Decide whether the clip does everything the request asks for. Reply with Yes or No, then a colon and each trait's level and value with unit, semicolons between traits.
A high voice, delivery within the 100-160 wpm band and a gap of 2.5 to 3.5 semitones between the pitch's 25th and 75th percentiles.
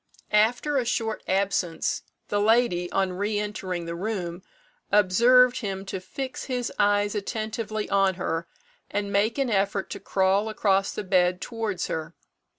Yes: high, 205 Hz; average, 150 wpm; average, 2.8 semitones